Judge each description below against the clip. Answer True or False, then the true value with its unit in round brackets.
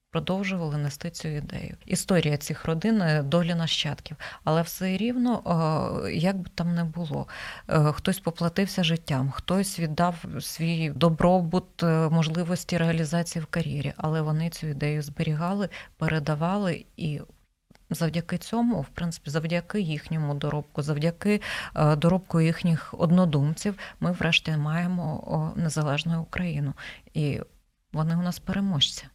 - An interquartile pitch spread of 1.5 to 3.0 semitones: True (2.4 semitones)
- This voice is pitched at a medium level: True (165 Hz)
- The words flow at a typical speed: True (115 wpm)